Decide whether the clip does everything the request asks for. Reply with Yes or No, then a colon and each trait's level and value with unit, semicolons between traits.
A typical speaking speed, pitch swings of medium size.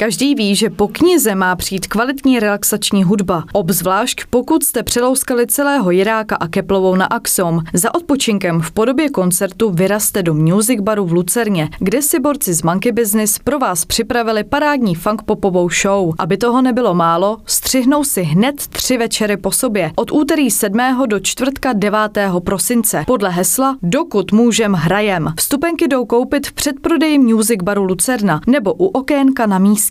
Yes: average, 160 wpm; average, 4.9 semitones